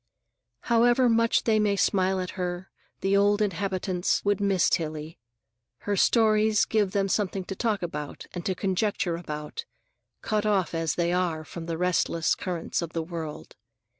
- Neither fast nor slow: Yes, average, 160 wpm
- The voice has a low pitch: No, medium, 185 Hz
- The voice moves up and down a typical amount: Yes, average, 3.4 semitones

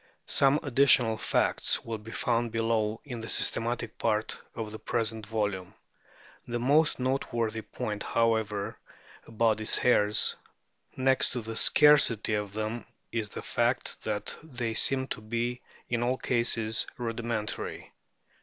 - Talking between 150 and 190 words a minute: No, slow, 135 wpm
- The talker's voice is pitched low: Yes, low, 115 Hz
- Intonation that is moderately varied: No, narrow, 2.0 semitones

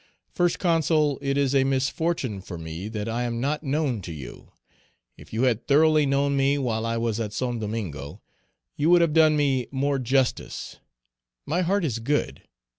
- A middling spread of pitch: Yes, average, 4.7 semitones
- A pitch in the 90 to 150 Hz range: Yes, low, 135 Hz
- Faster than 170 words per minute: Yes, average, 180 wpm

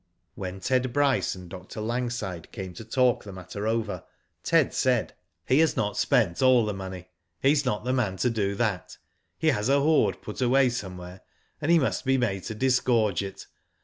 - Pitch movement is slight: No, average, 5.1 semitones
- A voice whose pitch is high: No, low, 110 Hz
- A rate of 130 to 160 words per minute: No, average, 190 wpm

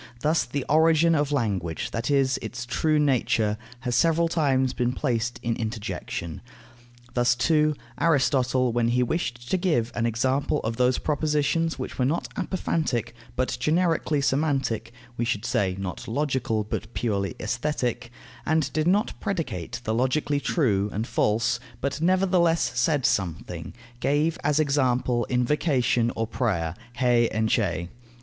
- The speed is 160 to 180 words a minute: No, average, 140 wpm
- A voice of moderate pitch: No, low, 130 Hz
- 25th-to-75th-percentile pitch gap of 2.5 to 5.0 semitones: Yes, average, 4.5 semitones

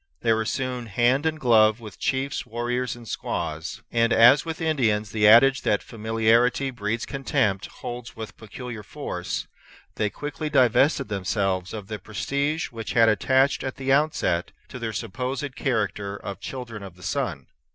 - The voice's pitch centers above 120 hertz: No, low, 115 Hz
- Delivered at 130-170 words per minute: Yes, average, 160 wpm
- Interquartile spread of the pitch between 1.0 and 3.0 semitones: No, average, 3.9 semitones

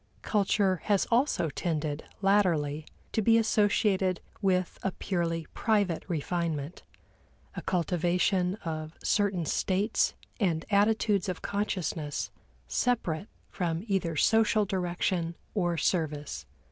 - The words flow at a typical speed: No, slow, 105 wpm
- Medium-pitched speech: Yes, medium, 180 Hz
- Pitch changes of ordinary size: Yes, average, 3.6 semitones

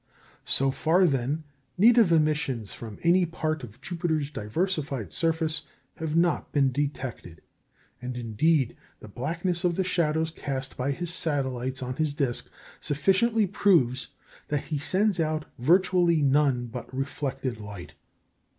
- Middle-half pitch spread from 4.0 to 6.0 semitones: Yes, average, 4.5 semitones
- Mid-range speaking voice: Yes, medium, 150 Hz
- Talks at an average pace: No, slow, 130 wpm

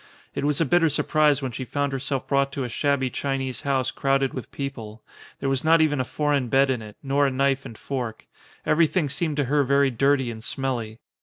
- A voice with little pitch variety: Yes, narrow, 1.9 semitones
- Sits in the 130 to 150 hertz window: Yes, low, 135 Hz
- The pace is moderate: No, fast, 215 wpm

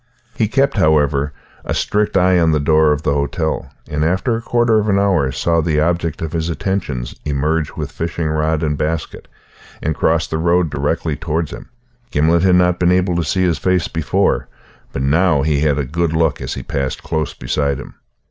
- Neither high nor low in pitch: No, very low, 80 Hz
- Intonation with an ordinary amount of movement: Yes, average, 3.0 semitones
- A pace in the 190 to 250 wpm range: Yes, average, 200 wpm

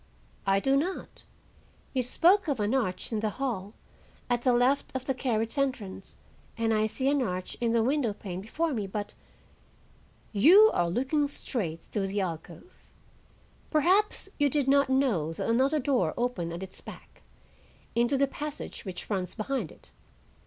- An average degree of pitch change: No, wide, 5.7 semitones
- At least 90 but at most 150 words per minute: No, average, 160 wpm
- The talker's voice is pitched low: No, high, 240 Hz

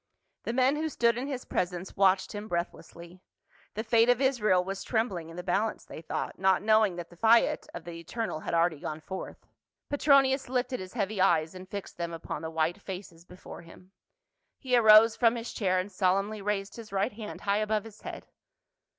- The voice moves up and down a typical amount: Yes, average, 4.3 semitones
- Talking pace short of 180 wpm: No, average, 195 wpm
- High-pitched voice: Yes, high, 200 Hz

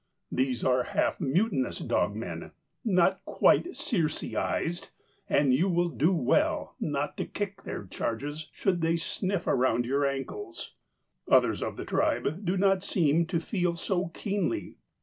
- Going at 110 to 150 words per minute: Yes, average, 145 wpm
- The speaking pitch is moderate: Yes, medium, 170 Hz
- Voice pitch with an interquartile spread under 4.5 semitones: No, average, 5.3 semitones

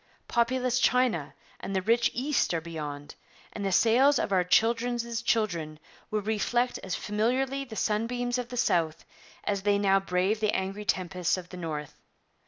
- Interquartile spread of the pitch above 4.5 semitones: Yes, average, 4.9 semitones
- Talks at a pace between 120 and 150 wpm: No, average, 165 wpm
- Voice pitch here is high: Yes, high, 210 Hz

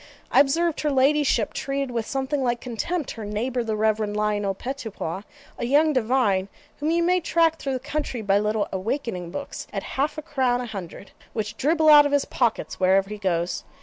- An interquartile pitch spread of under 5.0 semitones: No, wide, 5.5 semitones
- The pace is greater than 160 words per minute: Yes, average, 190 wpm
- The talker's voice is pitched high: Yes, high, 245 Hz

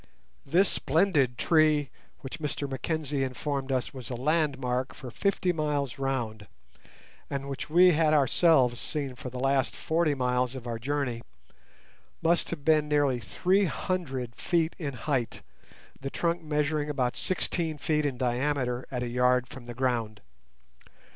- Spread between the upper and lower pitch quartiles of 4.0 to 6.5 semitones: No, average, 3.6 semitones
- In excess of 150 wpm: No, average, 145 wpm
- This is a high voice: No, medium, 140 Hz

